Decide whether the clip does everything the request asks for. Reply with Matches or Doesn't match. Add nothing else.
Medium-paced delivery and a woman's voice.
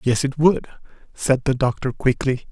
Doesn't match